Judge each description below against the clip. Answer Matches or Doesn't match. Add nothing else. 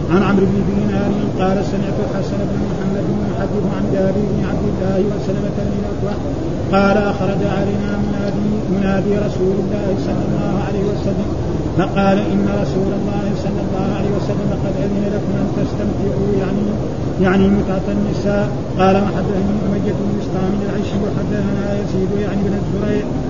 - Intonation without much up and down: Matches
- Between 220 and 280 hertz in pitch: Doesn't match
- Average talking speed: Doesn't match